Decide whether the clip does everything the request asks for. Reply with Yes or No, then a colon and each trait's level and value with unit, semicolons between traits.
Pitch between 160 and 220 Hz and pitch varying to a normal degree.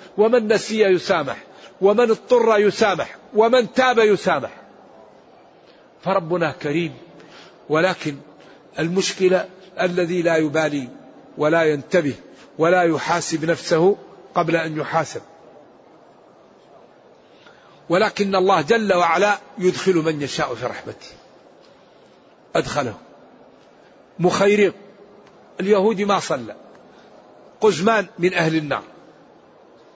Yes: medium, 185 Hz; average, 3.9 semitones